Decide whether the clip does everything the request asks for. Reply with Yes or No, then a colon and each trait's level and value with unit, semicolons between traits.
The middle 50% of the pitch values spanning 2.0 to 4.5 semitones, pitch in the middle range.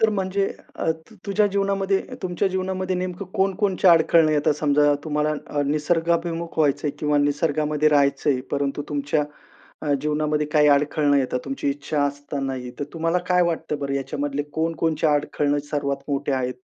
Yes: average, 3.0 semitones; medium, 150 Hz